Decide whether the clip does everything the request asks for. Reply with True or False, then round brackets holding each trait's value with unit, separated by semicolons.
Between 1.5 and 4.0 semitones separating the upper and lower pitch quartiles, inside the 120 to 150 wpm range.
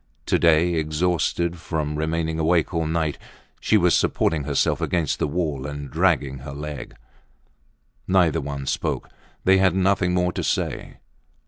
True (3.0 semitones; 145 wpm)